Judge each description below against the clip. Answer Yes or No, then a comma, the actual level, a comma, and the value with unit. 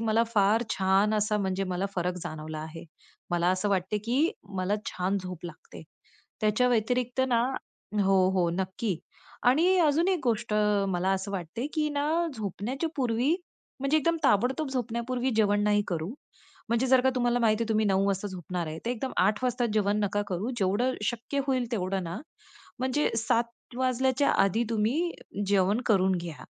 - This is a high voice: Yes, high, 215 Hz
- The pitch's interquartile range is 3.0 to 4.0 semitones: No, average, 4.8 semitones